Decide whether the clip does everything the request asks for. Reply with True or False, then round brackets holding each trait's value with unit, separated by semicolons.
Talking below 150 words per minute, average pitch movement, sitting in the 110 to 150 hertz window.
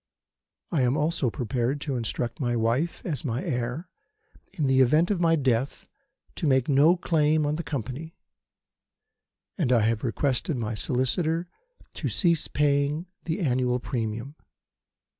True (140 wpm; 4.5 semitones; 140 Hz)